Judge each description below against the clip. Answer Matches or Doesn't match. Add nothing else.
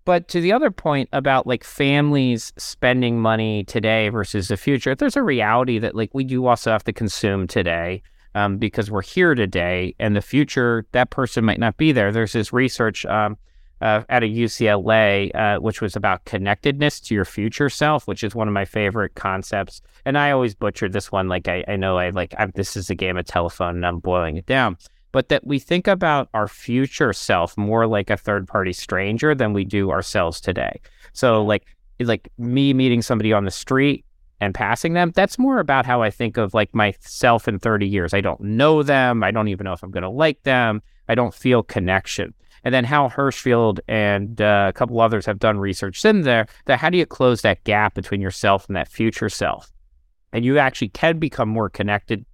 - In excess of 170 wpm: Matches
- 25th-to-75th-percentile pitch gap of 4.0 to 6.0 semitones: Matches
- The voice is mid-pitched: Doesn't match